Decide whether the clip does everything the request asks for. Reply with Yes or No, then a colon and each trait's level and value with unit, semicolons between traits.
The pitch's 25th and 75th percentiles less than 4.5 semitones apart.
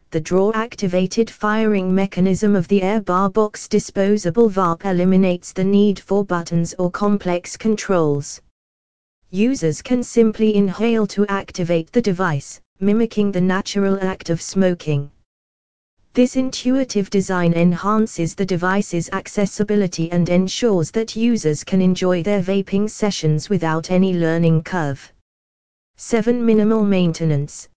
Yes: average, 3.5 semitones